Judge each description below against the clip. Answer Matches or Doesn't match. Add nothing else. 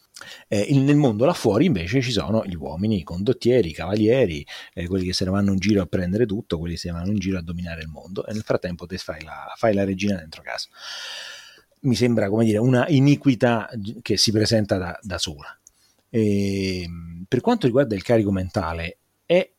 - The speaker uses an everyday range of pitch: Matches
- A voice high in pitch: Doesn't match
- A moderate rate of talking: Doesn't match